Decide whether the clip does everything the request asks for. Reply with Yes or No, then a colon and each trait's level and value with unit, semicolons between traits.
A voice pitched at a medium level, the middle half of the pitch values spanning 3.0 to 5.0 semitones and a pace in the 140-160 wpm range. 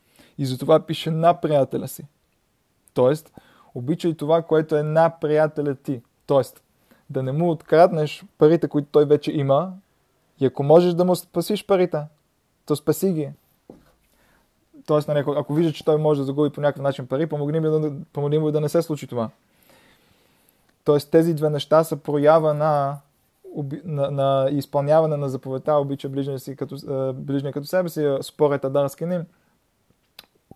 No: medium, 150 Hz; narrow, 2.4 semitones; average, 155 wpm